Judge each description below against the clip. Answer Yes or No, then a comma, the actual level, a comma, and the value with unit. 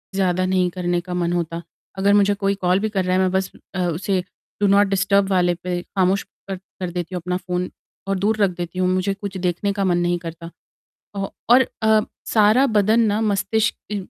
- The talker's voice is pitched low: No, high, 190 Hz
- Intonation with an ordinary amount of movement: No, narrow, 2.2 semitones